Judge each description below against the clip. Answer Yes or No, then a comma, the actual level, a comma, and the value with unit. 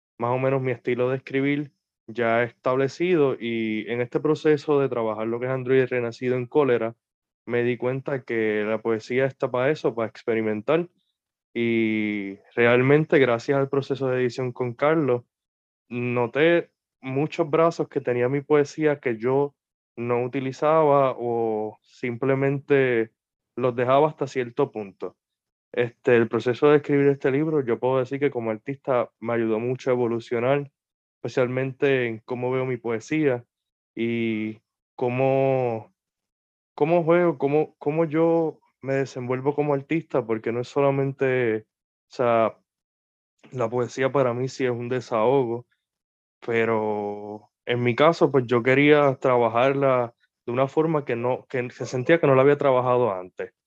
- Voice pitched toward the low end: Yes, low, 125 Hz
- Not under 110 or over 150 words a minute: Yes, average, 145 wpm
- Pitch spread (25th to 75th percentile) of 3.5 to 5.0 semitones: No, average, 3.0 semitones